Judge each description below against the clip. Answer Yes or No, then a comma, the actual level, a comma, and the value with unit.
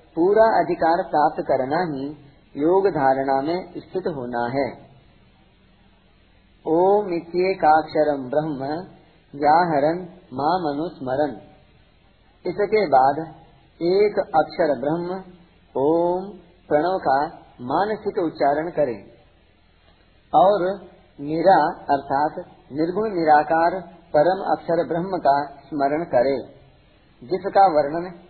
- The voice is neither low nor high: Yes, medium, 160 Hz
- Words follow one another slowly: Yes, slow, 85 wpm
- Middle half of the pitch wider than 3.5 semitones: Yes, average, 4.5 semitones